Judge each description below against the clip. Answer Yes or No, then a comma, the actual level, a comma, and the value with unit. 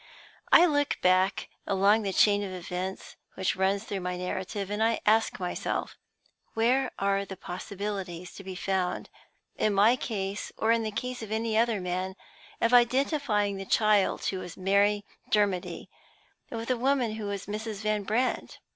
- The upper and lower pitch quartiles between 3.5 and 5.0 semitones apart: No, average, 2.8 semitones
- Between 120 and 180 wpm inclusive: Yes, average, 165 wpm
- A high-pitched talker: Yes, high, 205 Hz